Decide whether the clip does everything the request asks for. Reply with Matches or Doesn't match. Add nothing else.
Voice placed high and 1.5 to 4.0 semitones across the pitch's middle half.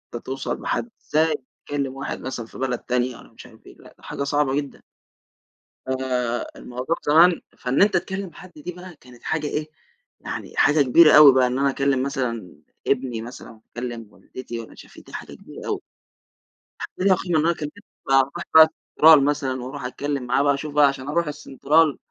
Doesn't match